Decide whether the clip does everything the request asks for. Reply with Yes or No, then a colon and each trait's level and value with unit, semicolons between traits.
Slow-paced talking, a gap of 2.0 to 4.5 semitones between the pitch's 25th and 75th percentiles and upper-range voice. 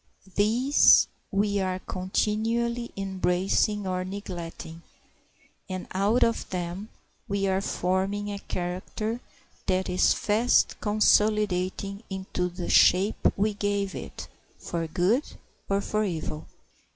Yes: slow, 110 wpm; narrow, 2.4 semitones; high, 195 Hz